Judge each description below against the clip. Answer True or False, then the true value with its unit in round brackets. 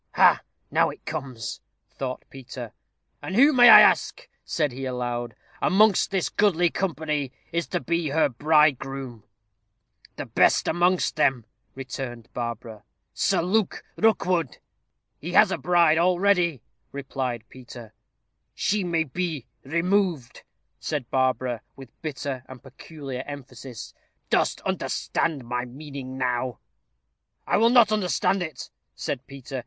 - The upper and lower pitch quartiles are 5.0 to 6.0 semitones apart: True (5.4 semitones)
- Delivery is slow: True (125 wpm)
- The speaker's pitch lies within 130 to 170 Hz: True (140 Hz)